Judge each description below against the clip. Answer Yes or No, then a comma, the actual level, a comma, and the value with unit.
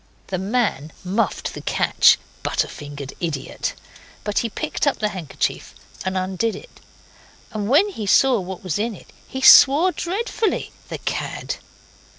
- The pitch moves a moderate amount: No, wide, 6.4 semitones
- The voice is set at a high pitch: Yes, high, 210 Hz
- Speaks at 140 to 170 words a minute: Yes, average, 150 wpm